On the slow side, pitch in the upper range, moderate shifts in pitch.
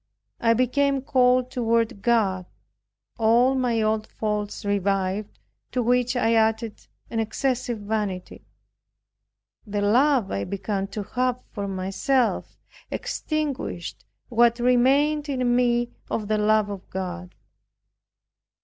Yes: slow, 115 wpm; high, 230 Hz; average, 3.6 semitones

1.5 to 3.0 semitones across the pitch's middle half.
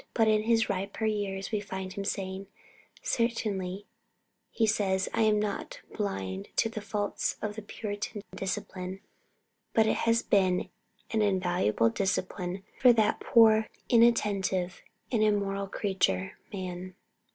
Yes: narrow, 2.4 semitones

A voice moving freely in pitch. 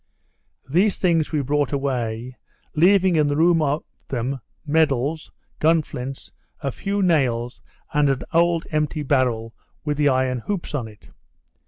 No: average, 3.9 semitones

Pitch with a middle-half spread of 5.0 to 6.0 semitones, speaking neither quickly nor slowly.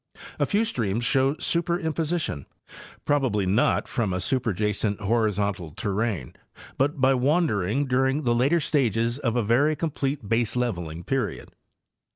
No: wide, 5.5 semitones; slow, 125 wpm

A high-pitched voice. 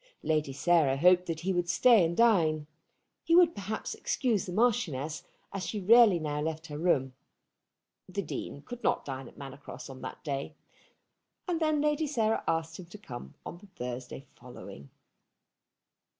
No: medium, 170 Hz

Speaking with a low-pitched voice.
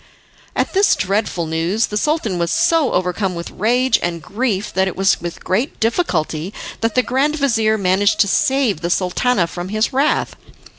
No: high, 205 Hz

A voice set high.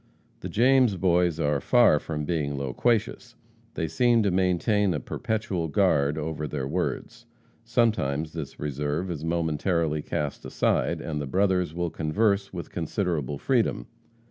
No: very low, 85 Hz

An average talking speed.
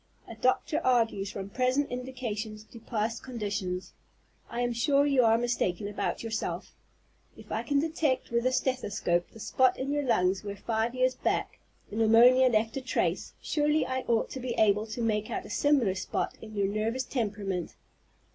Yes: average, 175 wpm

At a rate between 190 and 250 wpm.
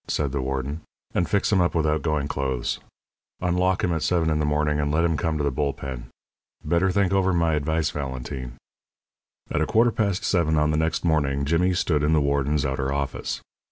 Yes: fast, 205 wpm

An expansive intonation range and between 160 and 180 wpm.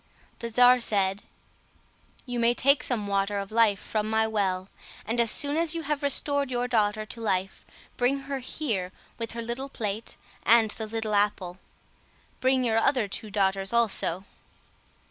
No: average, 3.5 semitones; average, 165 wpm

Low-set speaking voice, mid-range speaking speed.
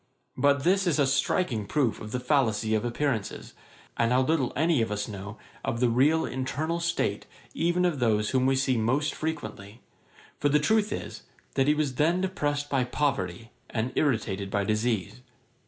Yes: low, 130 Hz; average, 175 wpm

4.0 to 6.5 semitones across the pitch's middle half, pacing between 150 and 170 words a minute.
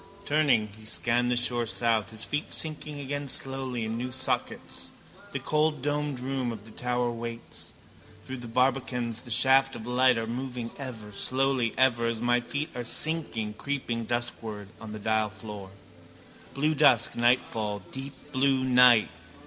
No: average, 2.8 semitones; average, 155 wpm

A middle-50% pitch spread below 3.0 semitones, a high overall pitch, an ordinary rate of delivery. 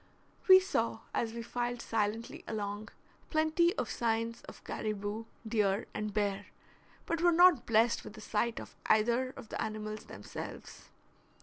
Yes: narrow, 2.4 semitones; high, 225 Hz; average, 145 wpm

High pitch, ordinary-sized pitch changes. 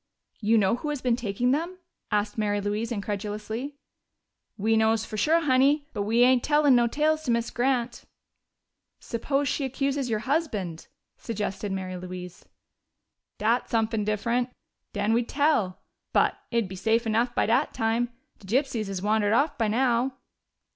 Yes: high, 230 Hz; average, 3.8 semitones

